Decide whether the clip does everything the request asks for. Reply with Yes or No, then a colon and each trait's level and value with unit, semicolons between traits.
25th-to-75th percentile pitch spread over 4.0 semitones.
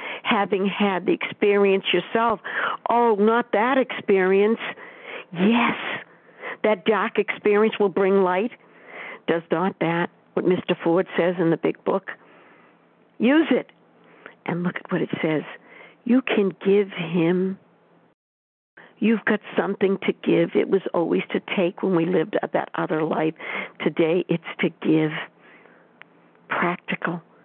No: average, 3.5 semitones